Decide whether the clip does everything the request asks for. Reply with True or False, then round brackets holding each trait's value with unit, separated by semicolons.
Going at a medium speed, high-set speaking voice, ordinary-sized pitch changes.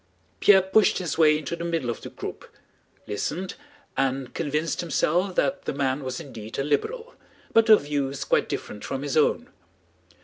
False (170 wpm; 150 Hz; 4.5 semitones)